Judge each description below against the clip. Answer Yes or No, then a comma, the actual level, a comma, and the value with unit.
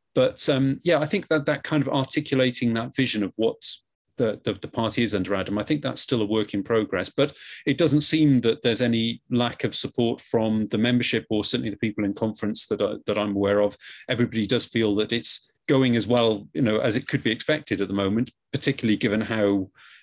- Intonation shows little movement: No, average, 3.9 semitones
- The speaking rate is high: Yes, fast, 225 wpm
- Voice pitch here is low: Yes, low, 115 Hz